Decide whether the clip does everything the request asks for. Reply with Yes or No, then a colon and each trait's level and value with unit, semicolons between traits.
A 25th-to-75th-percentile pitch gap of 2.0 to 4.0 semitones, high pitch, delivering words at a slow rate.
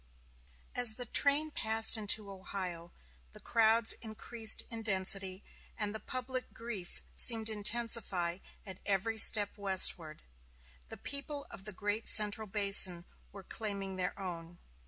Yes: average, 2.9 semitones; high, 210 Hz; slow, 130 wpm